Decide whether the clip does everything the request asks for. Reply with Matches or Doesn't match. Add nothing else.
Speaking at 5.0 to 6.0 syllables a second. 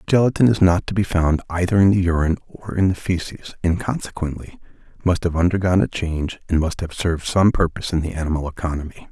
Doesn't match